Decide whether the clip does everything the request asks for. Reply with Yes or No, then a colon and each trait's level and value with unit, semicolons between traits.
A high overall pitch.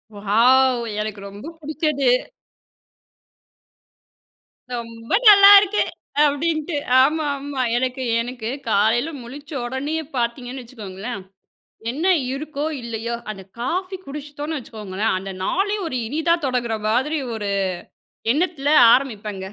Yes: very high, 260 Hz